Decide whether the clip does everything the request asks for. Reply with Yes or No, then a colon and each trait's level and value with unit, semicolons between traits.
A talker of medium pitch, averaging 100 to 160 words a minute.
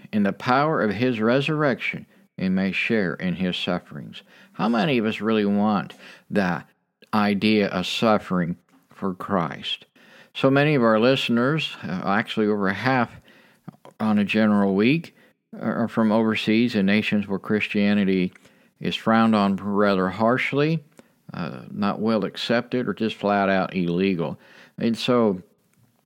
No: low, 110 Hz; slow, 135 wpm